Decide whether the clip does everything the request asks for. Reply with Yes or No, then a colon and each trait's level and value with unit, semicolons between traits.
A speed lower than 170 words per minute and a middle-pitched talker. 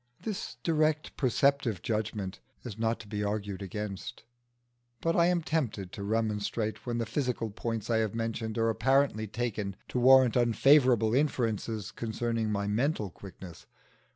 No: average, 145 wpm; low, 115 Hz